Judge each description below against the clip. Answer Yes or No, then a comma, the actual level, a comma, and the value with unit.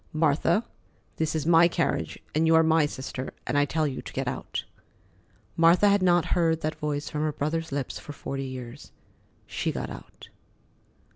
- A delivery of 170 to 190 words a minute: Yes, average, 175 wpm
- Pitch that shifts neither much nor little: No, narrow, 2.3 semitones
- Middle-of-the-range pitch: Yes, medium, 155 Hz